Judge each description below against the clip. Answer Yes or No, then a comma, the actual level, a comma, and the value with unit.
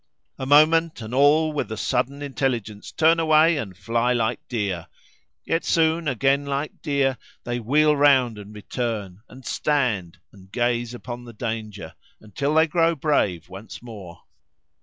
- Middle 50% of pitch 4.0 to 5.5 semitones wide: Yes, average, 5.2 semitones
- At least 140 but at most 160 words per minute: Yes, average, 150 wpm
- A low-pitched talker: Yes, low, 125 Hz